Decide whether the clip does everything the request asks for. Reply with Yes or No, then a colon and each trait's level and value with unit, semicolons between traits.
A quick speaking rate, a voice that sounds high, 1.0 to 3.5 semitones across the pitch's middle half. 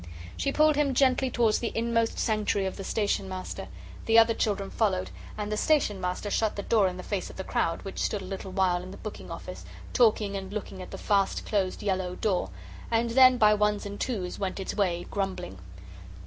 Yes: fast, 210 wpm; high, 205 Hz; average, 3.0 semitones